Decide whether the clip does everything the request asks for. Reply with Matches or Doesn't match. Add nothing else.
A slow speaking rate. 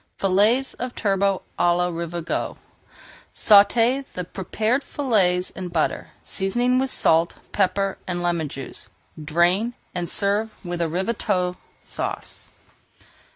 Matches